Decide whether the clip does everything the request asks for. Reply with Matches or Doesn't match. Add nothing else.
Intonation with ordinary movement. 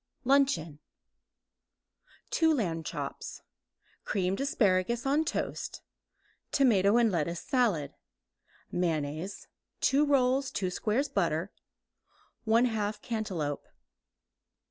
Doesn't match